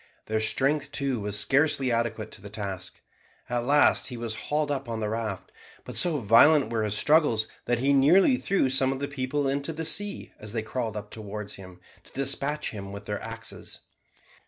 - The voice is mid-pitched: No, low, 125 Hz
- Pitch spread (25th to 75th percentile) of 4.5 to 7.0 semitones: Yes, average, 4.8 semitones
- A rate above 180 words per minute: Yes, average, 195 wpm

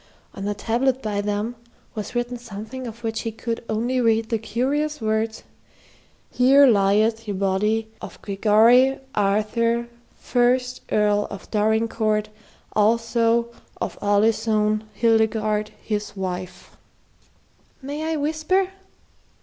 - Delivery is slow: Yes, slow, 115 wpm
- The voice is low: No, high, 225 Hz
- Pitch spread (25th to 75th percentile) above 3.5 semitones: No, narrow, 2.5 semitones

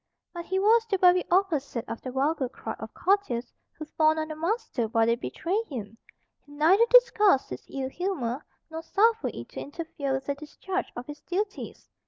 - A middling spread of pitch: No, wide, 6.5 semitones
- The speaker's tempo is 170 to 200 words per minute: Yes, average, 190 wpm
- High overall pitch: Yes, very high, 315 Hz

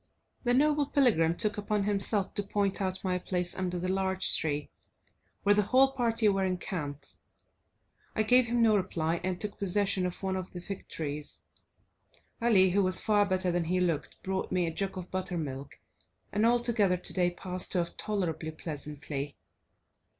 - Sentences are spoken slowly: No, average, 165 wpm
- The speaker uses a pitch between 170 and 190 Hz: Yes, medium, 185 Hz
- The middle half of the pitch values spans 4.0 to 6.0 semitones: No, average, 2.9 semitones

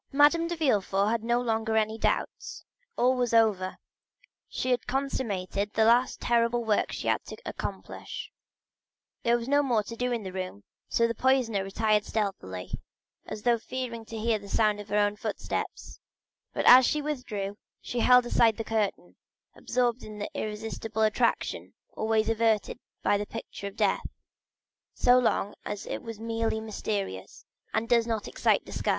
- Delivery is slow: No, average, 165 wpm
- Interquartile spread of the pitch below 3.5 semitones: Yes, narrow, 2.6 semitones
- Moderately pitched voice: No, high, 225 Hz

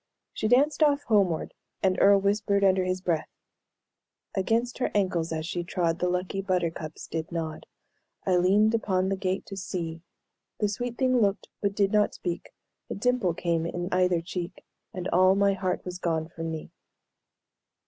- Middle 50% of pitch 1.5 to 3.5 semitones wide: Yes, average, 2.8 semitones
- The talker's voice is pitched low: No, medium, 185 Hz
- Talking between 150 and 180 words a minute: Yes, average, 170 wpm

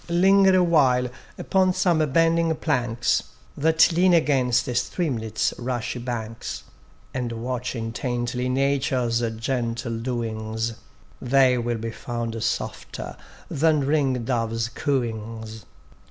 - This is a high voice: No, low, 125 Hz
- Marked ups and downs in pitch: No, average, 4.0 semitones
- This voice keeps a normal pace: No, slow, 105 wpm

